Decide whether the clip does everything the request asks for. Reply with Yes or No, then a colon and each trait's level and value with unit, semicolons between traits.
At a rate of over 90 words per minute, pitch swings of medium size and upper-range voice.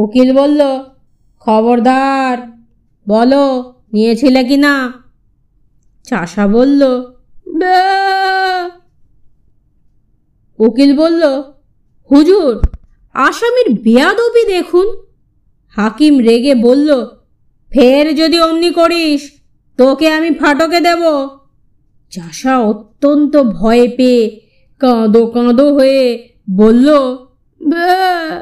No: average, 70 wpm; average, 4.9 semitones; very high, 275 Hz